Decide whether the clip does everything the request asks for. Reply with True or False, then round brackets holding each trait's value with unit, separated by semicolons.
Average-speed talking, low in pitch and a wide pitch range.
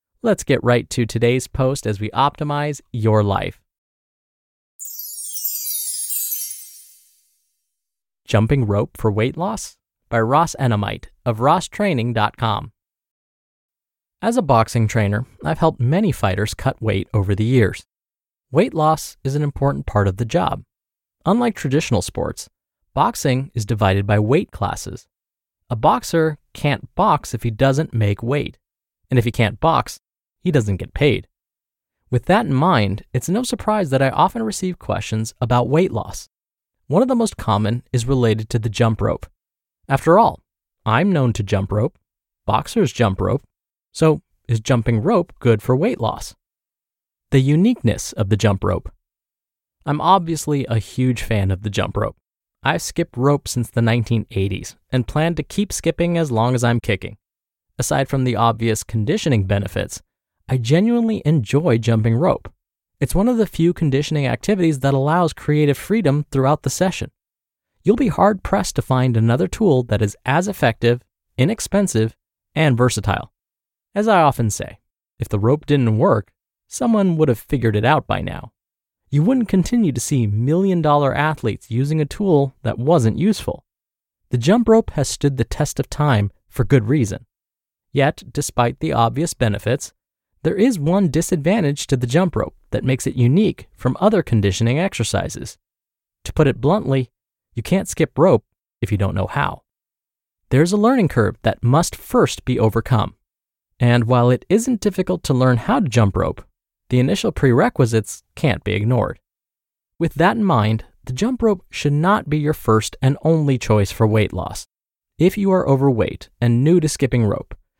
True (160 wpm; 125 Hz; 6.0 semitones)